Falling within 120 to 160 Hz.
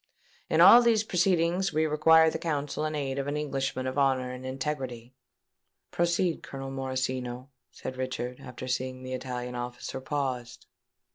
Yes: low, 135 Hz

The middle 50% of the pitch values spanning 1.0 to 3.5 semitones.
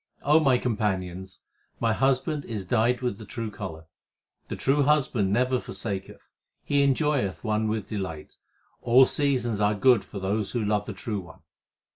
No: average, 4.5 semitones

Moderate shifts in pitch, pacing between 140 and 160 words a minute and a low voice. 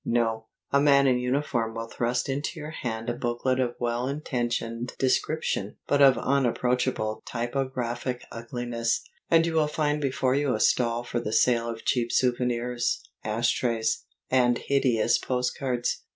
No: narrow, 2.3 semitones; average, 150 wpm; low, 125 Hz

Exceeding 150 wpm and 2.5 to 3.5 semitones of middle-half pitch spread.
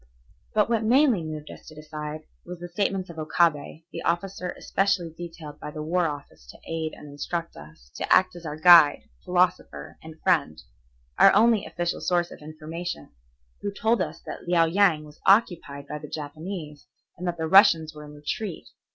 Yes: average, 180 wpm; average, 3.1 semitones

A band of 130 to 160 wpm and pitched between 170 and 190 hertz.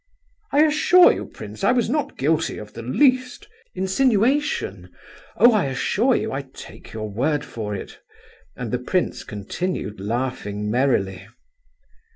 No: average, 140 wpm; medium, 140 Hz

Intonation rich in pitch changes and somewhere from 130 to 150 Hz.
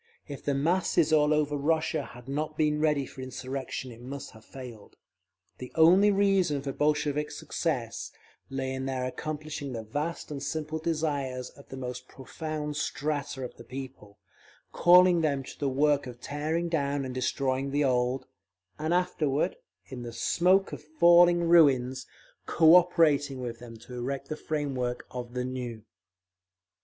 No: average, 3.2 semitones; medium, 140 Hz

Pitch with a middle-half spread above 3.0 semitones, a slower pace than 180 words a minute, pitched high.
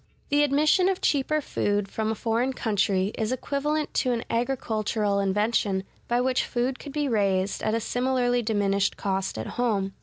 Yes: average, 4.4 semitones; average, 170 wpm; high, 230 Hz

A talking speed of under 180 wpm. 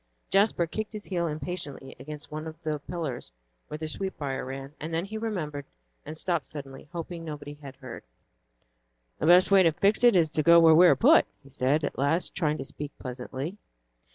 No: average, 190 wpm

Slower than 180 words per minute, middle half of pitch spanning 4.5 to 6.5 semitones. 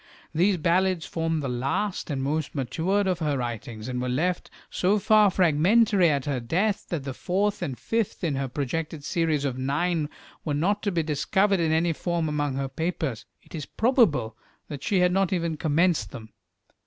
No: average, 185 wpm; average, 4.9 semitones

